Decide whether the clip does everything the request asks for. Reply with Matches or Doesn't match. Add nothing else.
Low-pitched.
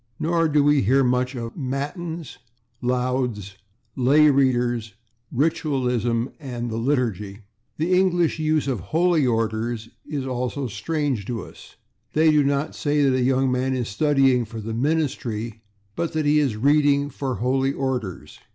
Matches